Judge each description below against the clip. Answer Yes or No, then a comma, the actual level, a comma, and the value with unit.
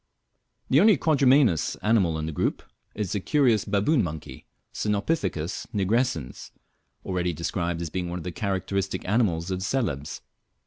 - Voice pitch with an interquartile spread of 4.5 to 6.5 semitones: Yes, average, 5.2 semitones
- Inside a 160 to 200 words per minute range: No, average, 140 wpm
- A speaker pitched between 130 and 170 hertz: No, very low, 95 Hz